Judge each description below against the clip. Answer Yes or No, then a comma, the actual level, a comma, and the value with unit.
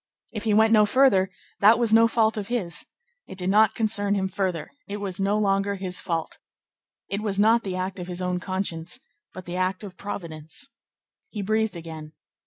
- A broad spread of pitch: No, average, 2.8 semitones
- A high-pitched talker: Yes, high, 195 Hz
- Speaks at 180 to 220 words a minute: Yes, average, 190 wpm